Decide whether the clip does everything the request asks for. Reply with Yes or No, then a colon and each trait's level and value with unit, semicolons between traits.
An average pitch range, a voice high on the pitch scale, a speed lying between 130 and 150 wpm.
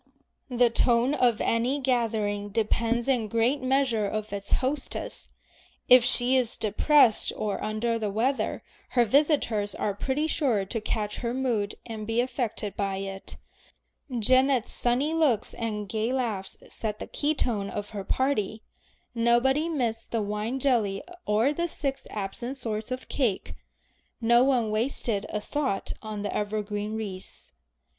Yes: average, 3.6 semitones; high, 230 Hz; average, 145 wpm